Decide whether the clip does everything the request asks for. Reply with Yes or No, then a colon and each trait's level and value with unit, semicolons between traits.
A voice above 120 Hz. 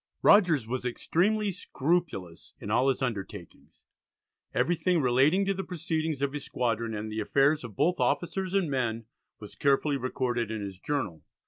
Yes: low, 135 Hz